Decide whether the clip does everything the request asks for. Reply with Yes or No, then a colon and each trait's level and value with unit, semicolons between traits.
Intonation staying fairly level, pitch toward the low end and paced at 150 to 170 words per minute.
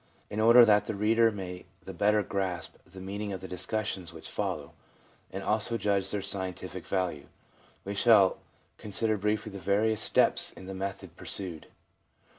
Yes: narrow, 2.2 semitones; low, 100 Hz; average, 165 wpm